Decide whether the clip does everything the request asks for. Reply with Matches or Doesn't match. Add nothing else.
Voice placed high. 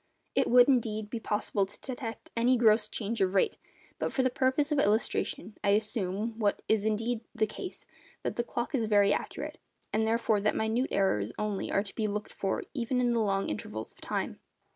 Matches